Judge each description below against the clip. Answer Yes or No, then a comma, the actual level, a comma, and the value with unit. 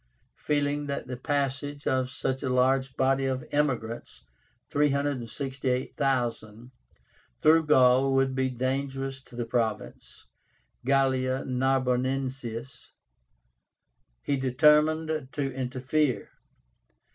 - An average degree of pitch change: No, narrow, 1.8 semitones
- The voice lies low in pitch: Yes, low, 130 Hz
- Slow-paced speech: Yes, slow, 90 wpm